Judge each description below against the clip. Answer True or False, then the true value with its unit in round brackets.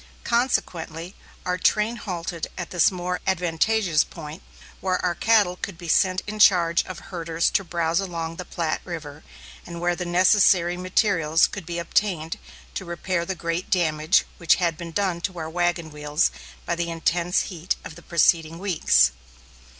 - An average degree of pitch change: False (1.9 semitones)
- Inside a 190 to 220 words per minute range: False (165 wpm)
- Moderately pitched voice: True (175 Hz)